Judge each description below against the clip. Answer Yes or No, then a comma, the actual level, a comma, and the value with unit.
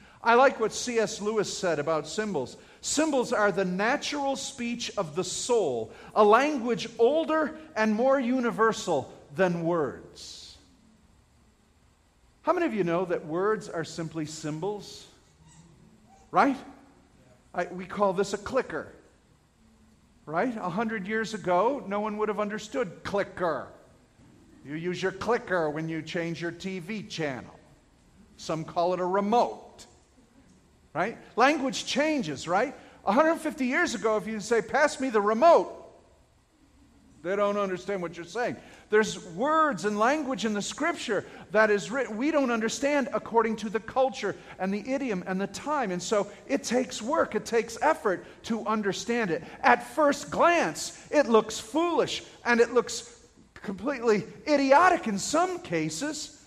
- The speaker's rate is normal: Yes, average, 145 wpm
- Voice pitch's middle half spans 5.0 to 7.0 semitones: Yes, wide, 5.4 semitones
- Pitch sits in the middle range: No, high, 220 Hz